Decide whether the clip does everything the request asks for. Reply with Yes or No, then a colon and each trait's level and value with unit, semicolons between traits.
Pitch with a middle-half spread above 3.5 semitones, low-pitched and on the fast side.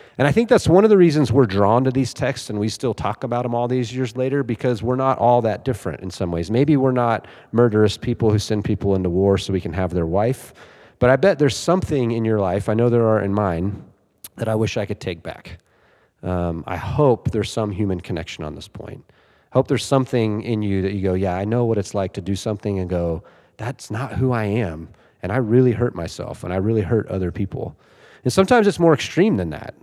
Yes: average, 4.5 semitones; low, 110 Hz; fast, 245 wpm